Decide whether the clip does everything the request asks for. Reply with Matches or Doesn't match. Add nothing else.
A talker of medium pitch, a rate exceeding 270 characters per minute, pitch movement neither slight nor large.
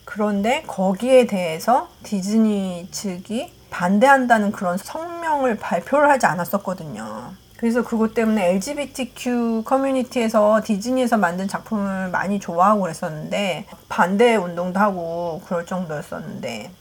Doesn't match